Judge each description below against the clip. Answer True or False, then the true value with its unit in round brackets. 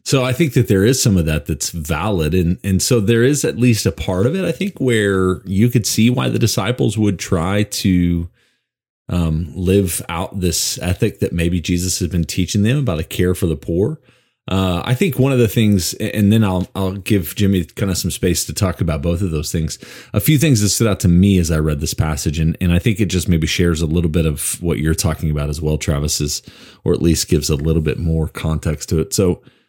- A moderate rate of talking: False (245 wpm)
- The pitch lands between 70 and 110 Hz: True (90 Hz)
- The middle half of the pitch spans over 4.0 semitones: True (4.6 semitones)